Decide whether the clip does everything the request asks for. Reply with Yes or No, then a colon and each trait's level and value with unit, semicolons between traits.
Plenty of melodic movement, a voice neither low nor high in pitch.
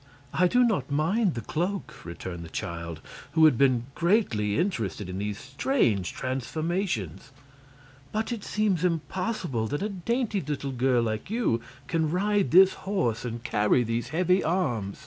Yes: wide, 8.8 semitones; medium, 150 Hz